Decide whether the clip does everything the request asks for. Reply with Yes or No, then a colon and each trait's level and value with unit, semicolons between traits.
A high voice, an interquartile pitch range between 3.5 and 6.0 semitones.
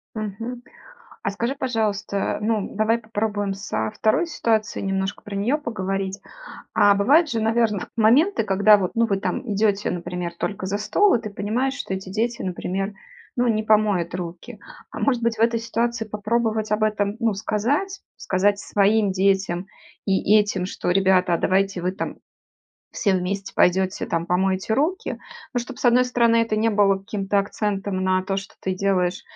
No: high, 205 Hz; average, 2.9 semitones